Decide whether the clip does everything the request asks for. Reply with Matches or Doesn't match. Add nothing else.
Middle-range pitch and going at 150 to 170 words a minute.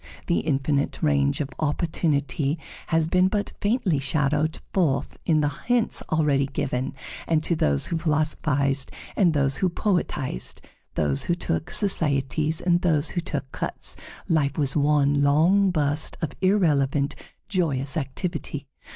Doesn't match